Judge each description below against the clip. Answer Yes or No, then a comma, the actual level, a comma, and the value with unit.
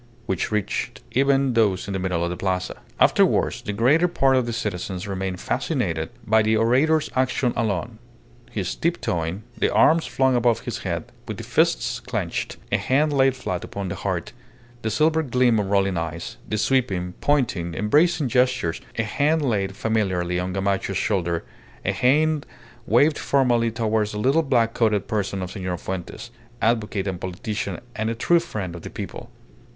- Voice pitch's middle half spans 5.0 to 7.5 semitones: Yes, average, 5.3 semitones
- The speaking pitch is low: Yes, low, 110 Hz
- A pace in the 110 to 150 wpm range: No, average, 170 wpm